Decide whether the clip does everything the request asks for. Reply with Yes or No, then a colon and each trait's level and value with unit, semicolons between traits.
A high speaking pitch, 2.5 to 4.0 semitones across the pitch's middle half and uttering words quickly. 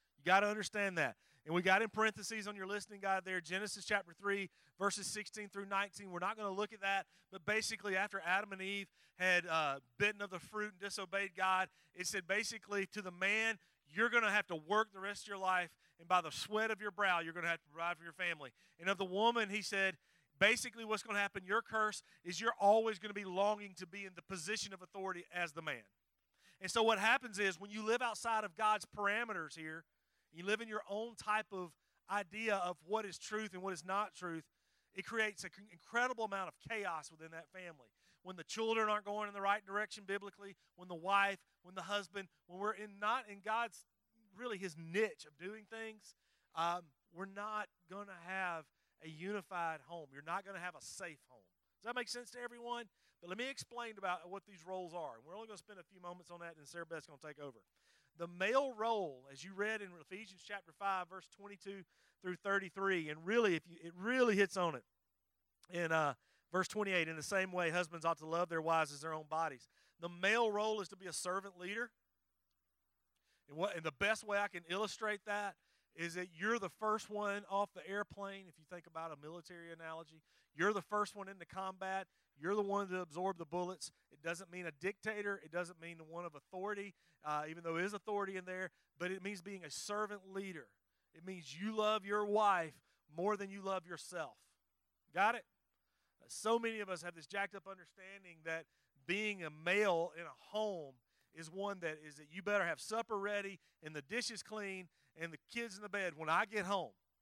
Yes: high, 195 Hz; average, 3.5 semitones; fast, 215 wpm